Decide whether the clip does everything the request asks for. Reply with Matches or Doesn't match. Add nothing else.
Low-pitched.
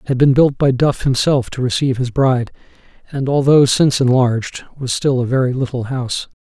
Matches